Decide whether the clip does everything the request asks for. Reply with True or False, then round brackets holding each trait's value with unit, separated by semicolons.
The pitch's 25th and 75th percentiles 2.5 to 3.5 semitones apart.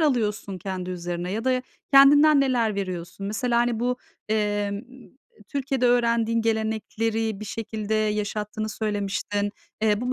True (2.9 semitones)